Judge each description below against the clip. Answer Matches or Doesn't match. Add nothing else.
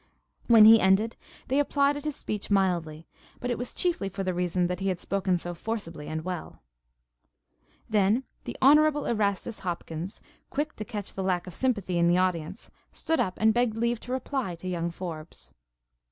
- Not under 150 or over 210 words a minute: Matches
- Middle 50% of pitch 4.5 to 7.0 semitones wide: Matches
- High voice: Matches